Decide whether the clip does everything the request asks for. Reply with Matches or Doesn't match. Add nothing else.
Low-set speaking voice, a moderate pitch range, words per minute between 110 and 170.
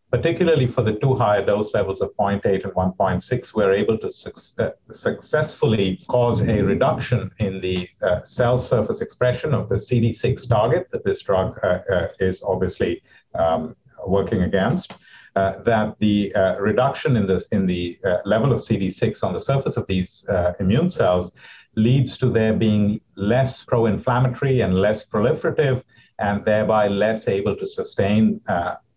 Matches